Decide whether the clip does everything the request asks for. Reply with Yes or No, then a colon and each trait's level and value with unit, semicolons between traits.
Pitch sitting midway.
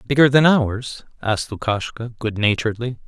No: low, 120 Hz